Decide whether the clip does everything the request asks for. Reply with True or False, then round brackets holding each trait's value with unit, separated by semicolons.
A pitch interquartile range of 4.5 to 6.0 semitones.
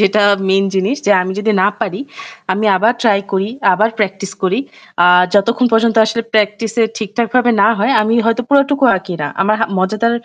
False (2.8 semitones)